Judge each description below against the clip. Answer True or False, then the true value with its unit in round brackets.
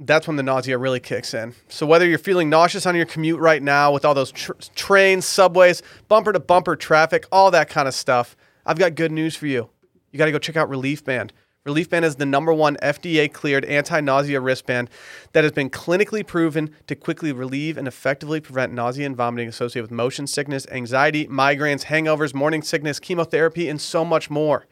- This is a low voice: False (150 Hz)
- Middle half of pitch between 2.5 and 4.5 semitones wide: True (3.4 semitones)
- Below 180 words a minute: False (205 wpm)